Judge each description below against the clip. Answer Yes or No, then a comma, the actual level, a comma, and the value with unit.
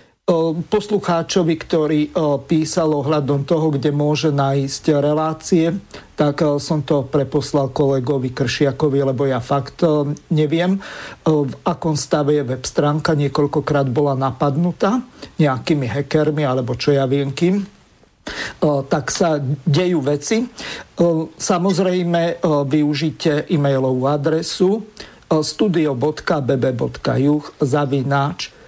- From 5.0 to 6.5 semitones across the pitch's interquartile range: No, average, 2.8 semitones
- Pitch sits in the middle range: Yes, medium, 150 Hz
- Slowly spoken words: Yes, slow, 95 wpm